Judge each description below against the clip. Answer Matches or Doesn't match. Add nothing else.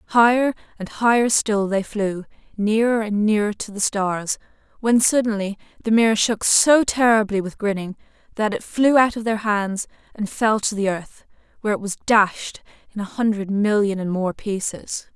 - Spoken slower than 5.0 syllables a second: Matches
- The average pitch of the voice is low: Doesn't match